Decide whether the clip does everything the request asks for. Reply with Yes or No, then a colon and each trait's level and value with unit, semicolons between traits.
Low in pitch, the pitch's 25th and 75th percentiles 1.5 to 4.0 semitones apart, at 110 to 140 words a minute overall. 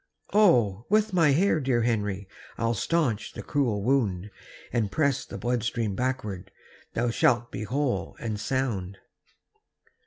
No: low, 120 Hz; average, 4.7 semitones; slow, 135 wpm